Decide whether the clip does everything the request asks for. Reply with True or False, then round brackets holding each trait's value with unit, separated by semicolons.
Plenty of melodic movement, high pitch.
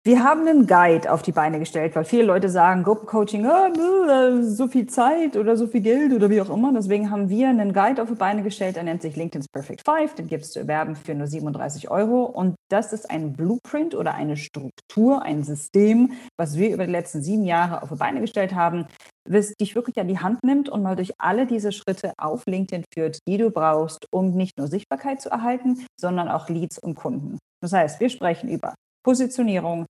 True (6.2 semitones; 200 Hz)